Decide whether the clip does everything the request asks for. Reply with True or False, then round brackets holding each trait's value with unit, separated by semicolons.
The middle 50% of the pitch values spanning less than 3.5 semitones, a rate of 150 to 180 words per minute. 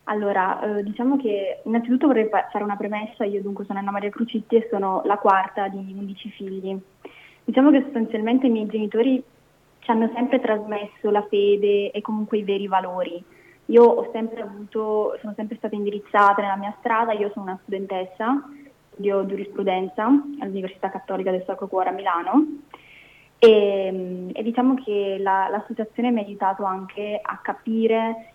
True (2.5 semitones; 160 wpm)